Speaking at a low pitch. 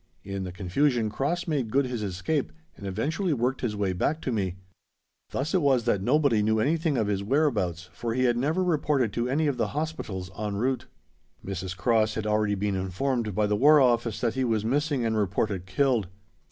Yes: low, 115 Hz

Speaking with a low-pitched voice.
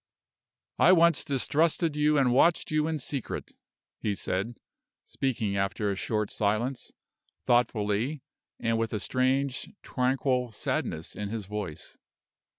Yes: low, 125 Hz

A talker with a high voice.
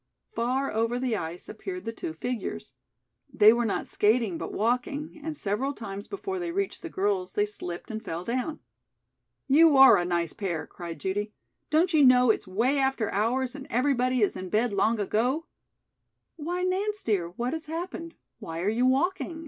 Yes: high, 240 Hz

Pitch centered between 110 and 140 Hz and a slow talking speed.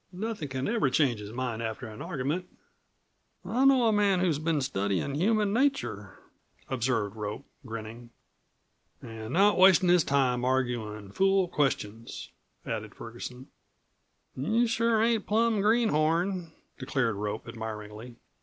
Yes: low, 135 Hz; slow, 125 wpm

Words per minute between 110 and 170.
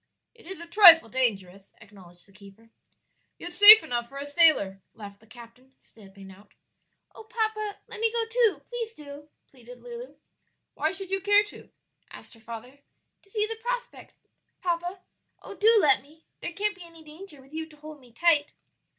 No: average, 180 wpm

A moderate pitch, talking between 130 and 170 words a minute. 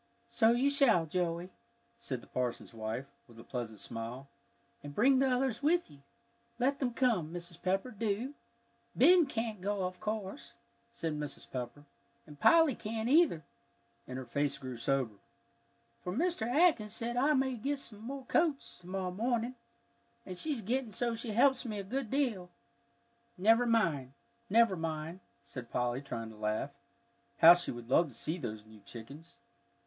No: high, 200 Hz; average, 160 wpm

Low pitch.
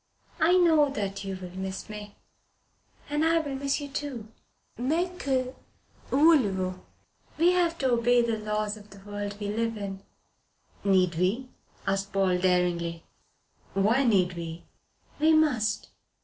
No: high, 215 Hz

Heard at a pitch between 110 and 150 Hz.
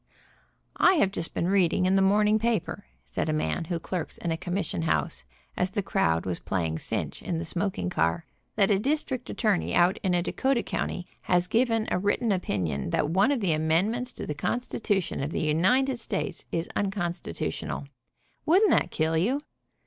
No: medium, 185 Hz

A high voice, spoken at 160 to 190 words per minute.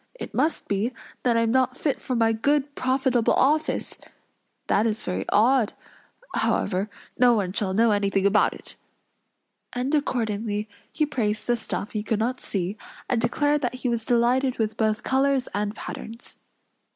Yes: high, 230 Hz; average, 165 wpm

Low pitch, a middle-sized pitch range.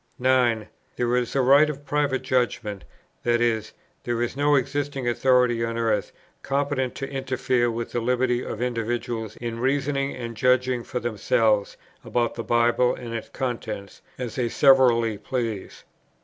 No: low, 120 Hz; narrow, 2.1 semitones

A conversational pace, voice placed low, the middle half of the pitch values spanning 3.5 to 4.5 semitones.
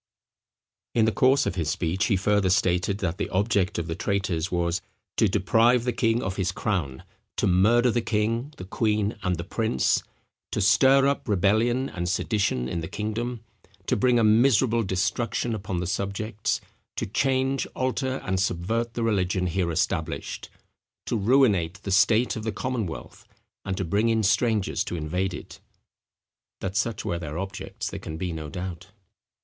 Yes: average, 170 wpm; low, 100 Hz; average, 4.1 semitones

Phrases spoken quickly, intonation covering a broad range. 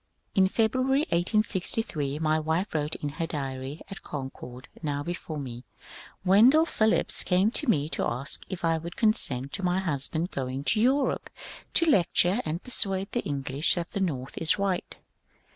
No: average, 170 wpm; wide, 5.7 semitones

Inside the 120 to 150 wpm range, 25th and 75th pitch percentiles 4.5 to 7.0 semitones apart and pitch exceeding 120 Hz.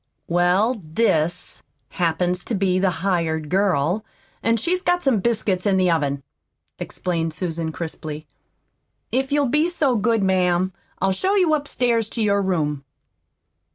Yes: average, 140 wpm; wide, 5.4 semitones; high, 190 Hz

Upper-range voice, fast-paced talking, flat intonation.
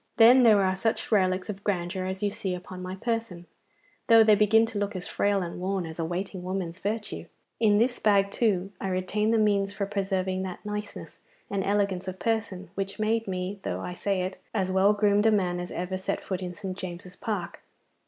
Yes: high, 195 Hz; fast, 210 wpm; narrow, 2.3 semitones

